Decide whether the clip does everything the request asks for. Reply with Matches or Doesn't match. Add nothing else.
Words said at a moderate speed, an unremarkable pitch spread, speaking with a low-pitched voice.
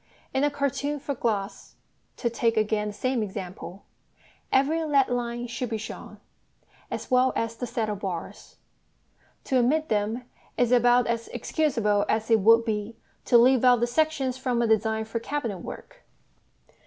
Doesn't match